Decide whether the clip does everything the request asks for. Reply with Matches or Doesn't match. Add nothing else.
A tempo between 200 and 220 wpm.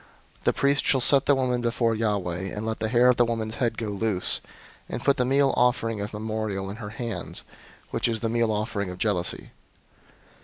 Matches